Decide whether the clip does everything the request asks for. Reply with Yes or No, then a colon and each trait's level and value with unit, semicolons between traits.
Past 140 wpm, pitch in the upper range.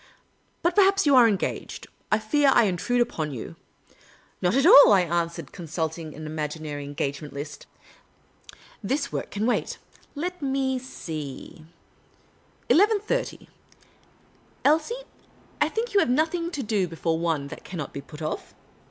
Yes: average, 155 wpm; high, 195 Hz